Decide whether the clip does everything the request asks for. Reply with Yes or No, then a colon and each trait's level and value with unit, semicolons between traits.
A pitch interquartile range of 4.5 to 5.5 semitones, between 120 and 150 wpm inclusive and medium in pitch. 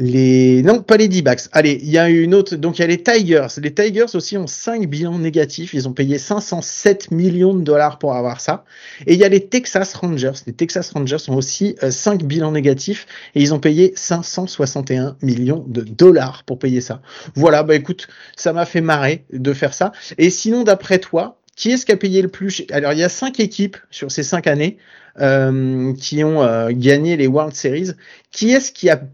No: average, 5.1 semitones; average, 215 wpm; medium, 160 Hz